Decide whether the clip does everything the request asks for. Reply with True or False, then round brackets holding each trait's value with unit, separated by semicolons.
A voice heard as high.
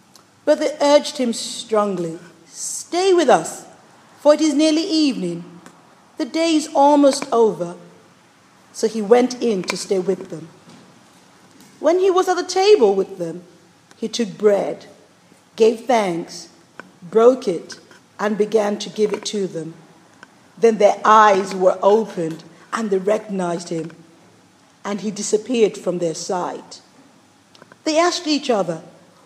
True (210 Hz)